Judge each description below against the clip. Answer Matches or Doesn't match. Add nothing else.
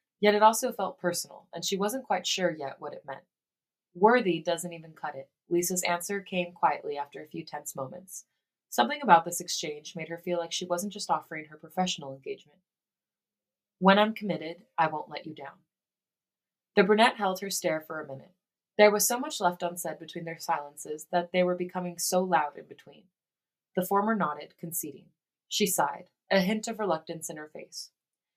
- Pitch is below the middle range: Doesn't match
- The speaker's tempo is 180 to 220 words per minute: Matches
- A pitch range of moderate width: Matches